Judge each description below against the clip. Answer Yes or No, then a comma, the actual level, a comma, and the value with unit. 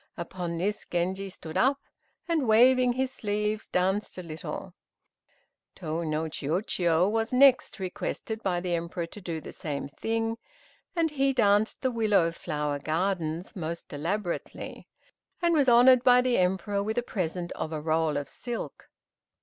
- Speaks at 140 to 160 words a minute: Yes, average, 150 wpm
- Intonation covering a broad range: Yes, wide, 5.8 semitones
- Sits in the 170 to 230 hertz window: Yes, high, 190 Hz